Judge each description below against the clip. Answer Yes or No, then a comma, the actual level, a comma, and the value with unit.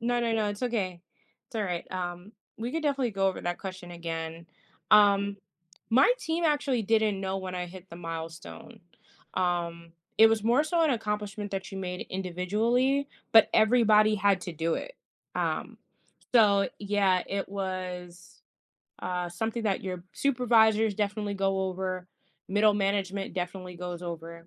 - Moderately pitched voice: No, high, 195 Hz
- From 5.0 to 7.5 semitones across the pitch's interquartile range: No, average, 3.5 semitones